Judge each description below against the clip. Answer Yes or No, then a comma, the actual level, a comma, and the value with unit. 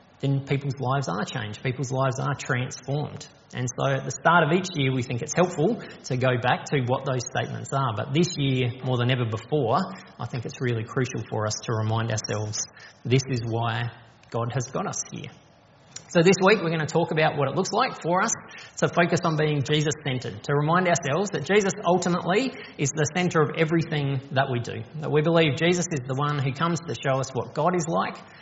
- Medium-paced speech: No, fast, 220 wpm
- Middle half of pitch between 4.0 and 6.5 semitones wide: Yes, average, 4.4 semitones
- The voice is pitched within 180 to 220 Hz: No, medium, 140 Hz